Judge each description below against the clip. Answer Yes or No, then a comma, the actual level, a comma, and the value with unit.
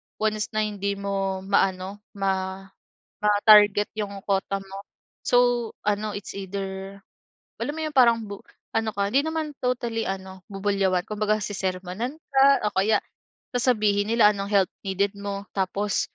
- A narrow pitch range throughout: Yes, narrow, 1.9 semitones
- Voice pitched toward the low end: No, high, 200 Hz